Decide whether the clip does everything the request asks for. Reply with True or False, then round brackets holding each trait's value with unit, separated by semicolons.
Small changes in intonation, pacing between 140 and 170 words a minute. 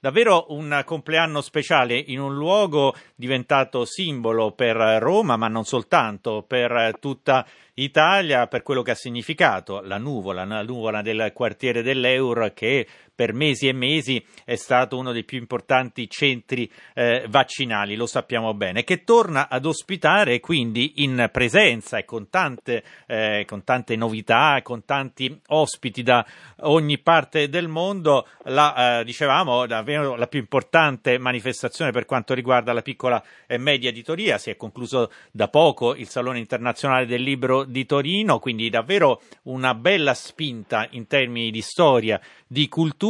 False (3.5 semitones; 150 wpm)